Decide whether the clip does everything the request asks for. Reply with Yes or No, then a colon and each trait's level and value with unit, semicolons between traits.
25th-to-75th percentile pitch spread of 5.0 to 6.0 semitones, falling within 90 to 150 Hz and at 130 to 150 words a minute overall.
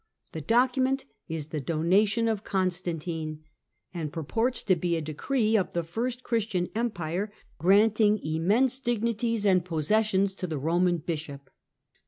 No: wide, 5.5 semitones; high, 190 Hz; slow, 135 wpm